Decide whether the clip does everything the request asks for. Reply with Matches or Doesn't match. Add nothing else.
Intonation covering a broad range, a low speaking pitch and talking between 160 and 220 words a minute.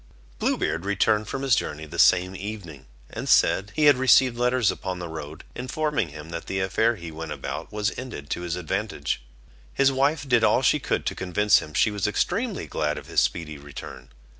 Matches